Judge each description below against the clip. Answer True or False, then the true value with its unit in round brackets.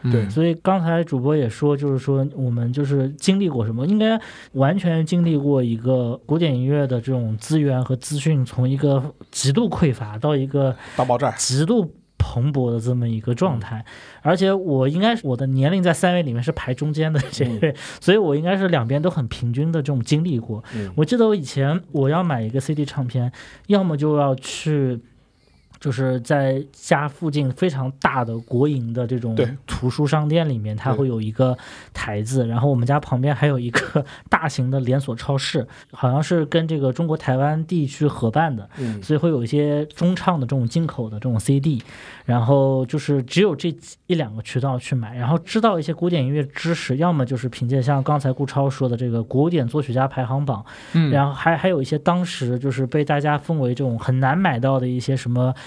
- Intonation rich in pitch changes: False (3.7 semitones)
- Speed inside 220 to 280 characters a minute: False (305 characters per minute)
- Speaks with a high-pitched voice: False (140 Hz)